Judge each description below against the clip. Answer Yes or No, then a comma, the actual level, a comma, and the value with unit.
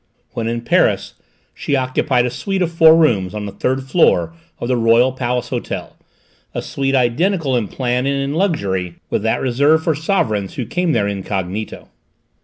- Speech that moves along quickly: No, average, 175 wpm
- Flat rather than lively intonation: No, average, 5.3 semitones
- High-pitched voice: No, low, 125 Hz